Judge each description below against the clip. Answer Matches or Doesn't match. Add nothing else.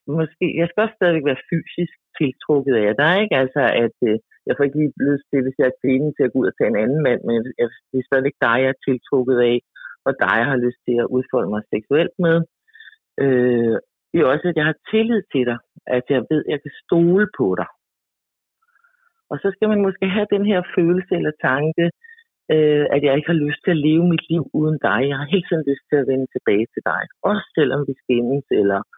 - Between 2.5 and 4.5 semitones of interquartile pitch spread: Doesn't match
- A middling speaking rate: Doesn't match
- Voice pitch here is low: Doesn't match